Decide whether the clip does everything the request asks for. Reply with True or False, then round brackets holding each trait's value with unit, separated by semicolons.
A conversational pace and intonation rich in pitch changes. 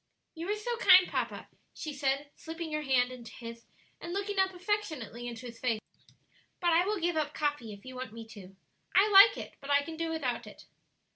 False (210 wpm; 6.6 semitones)